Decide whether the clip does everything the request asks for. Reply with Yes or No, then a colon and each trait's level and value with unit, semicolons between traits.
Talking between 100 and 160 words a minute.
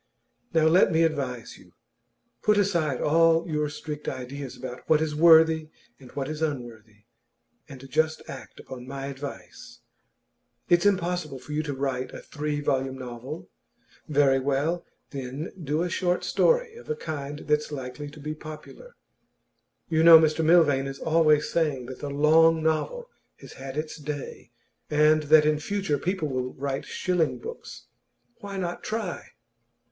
Yes: average, 155 wpm